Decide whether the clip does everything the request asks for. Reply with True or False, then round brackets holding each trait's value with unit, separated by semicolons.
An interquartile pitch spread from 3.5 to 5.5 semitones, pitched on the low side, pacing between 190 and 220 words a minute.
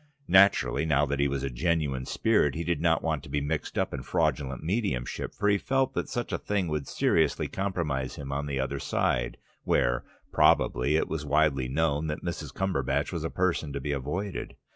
True (3.9 semitones; 75 Hz; 200 wpm)